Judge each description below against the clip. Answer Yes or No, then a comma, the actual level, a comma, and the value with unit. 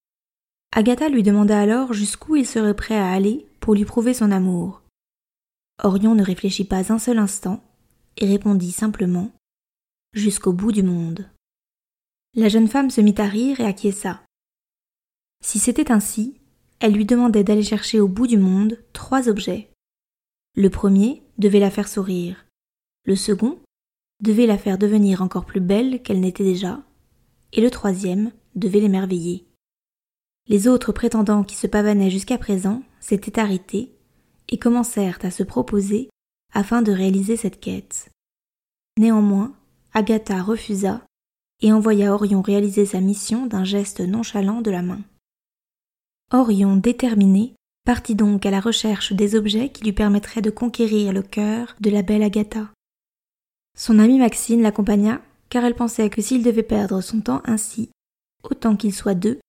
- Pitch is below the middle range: No, high, 210 Hz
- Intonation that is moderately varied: No, narrow, 2.3 semitones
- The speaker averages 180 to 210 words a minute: No, average, 150 wpm